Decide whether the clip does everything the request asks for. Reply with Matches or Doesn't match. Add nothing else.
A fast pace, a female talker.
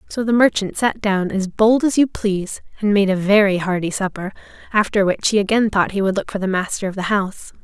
Matches